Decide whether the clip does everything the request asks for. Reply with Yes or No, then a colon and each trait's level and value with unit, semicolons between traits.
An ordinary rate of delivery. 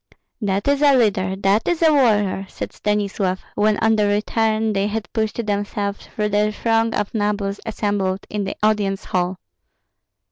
Yes: average, 165 wpm